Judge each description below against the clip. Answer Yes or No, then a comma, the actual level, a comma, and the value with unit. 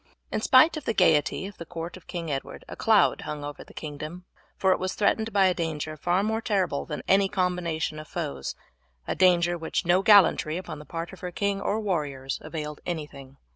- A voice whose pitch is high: No, medium, 175 Hz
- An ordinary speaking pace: No, fast, 210 wpm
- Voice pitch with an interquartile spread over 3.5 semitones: Yes, average, 4.0 semitones